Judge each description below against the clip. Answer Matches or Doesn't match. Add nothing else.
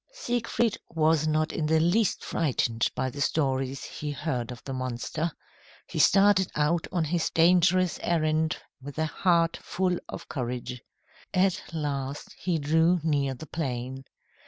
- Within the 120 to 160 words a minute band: Matches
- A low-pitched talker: Doesn't match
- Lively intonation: Doesn't match